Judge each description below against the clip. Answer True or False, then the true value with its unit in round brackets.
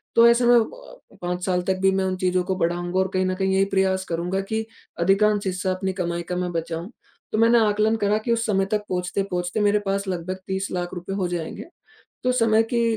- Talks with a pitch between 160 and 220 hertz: True (190 Hz)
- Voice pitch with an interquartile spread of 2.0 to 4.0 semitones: True (2.9 semitones)